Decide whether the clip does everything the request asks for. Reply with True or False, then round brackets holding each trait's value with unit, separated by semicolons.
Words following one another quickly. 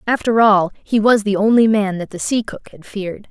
True (235 wpm)